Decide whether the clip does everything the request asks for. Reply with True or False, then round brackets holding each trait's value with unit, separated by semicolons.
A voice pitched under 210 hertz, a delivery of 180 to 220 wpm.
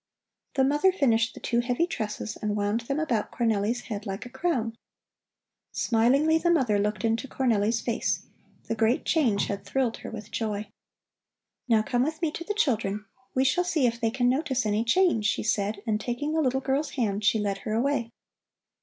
False (235 Hz; 190 wpm)